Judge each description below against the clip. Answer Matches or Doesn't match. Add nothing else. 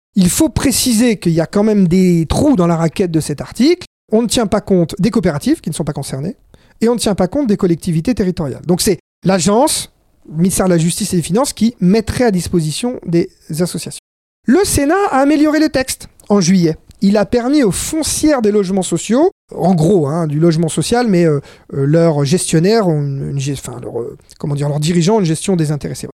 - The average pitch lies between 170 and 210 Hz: Matches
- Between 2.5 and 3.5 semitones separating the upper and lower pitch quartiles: Doesn't match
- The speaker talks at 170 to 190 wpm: Doesn't match